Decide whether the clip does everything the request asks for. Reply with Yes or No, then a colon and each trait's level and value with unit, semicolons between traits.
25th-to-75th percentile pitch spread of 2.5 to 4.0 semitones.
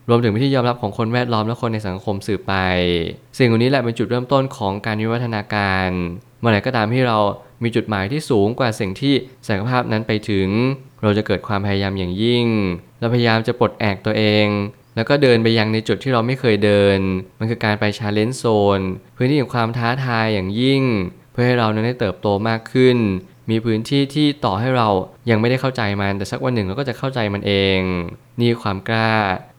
Yes: average, 3.4 semitones